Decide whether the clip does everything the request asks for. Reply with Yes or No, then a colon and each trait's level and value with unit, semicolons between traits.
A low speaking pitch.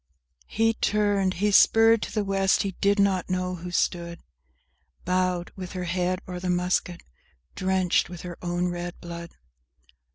No: medium, 185 Hz